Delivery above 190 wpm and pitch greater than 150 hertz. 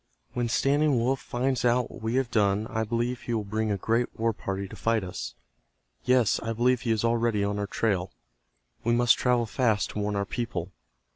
No: fast, 205 wpm; low, 115 Hz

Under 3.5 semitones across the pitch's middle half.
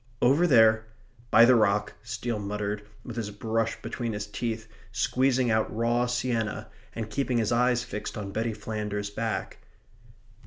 Yes: narrow, 2.4 semitones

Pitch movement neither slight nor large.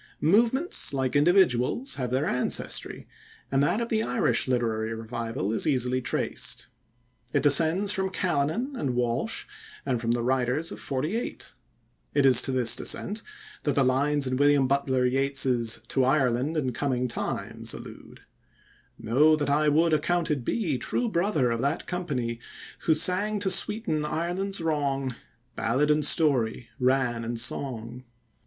Yes: average, 4.7 semitones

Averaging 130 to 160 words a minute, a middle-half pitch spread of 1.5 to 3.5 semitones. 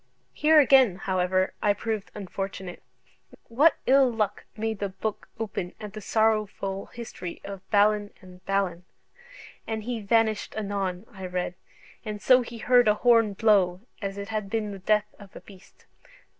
Yes: average, 155 wpm; narrow, 2.5 semitones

